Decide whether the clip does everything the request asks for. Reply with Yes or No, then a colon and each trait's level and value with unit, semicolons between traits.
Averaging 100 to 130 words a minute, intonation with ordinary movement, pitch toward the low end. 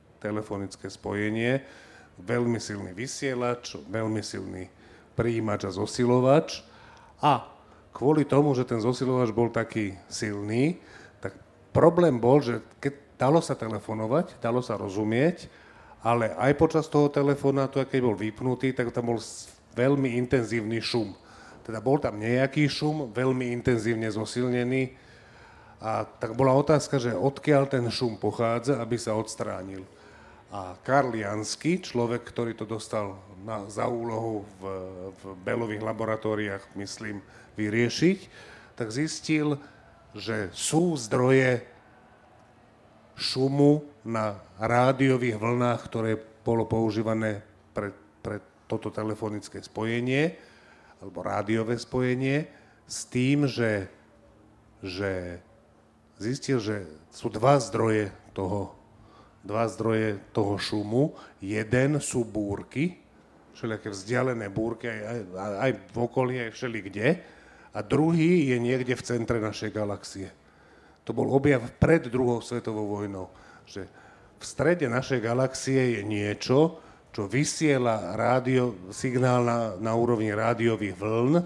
Yes: average, 115 wpm; average, 3.4 semitones; low, 115 Hz